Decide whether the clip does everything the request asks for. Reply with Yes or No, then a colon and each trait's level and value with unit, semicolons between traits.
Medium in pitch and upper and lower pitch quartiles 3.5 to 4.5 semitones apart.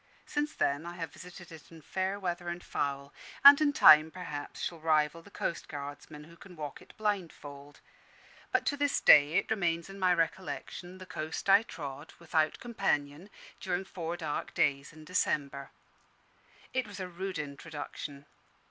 Yes: medium, 165 Hz; average, 4.0 semitones